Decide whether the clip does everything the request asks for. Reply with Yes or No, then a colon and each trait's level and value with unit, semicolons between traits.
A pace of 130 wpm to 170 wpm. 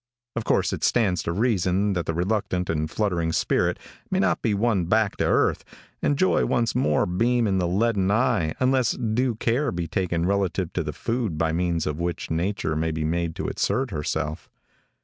No: average, 190 wpm